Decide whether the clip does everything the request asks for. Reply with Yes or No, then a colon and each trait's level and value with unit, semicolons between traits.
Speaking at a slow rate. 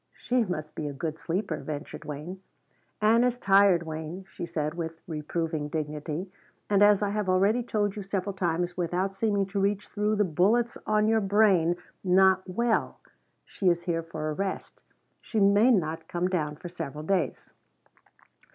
No: average, 170 wpm